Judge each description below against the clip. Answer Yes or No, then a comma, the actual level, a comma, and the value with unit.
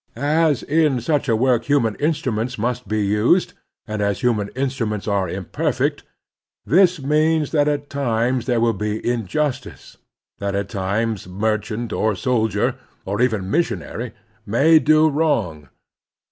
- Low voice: Yes, low, 120 Hz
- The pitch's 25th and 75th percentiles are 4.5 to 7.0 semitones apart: Yes, wide, 5.4 semitones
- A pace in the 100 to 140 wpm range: Yes, slow, 135 wpm